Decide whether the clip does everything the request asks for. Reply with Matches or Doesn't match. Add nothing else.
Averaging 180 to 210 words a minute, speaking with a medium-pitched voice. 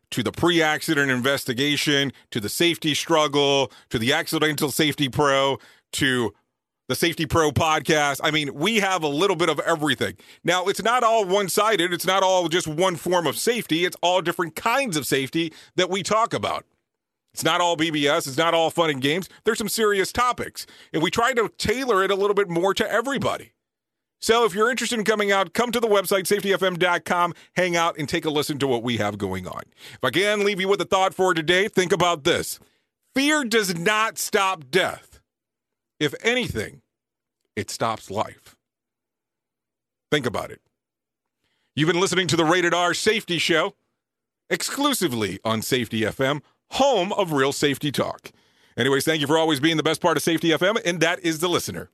Matches